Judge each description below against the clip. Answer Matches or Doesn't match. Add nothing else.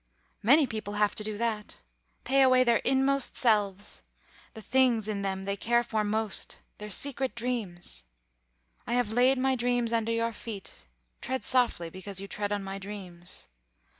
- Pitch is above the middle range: Matches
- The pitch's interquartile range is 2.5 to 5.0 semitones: Matches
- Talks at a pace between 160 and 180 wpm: Matches